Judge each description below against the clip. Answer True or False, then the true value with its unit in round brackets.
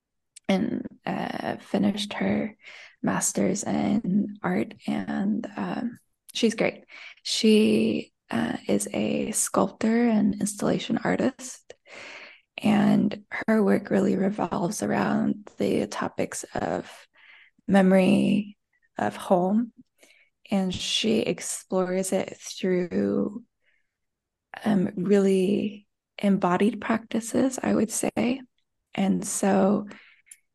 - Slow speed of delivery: True (90 wpm)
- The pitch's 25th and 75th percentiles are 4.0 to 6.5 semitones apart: False (3.2 semitones)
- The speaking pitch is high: True (210 Hz)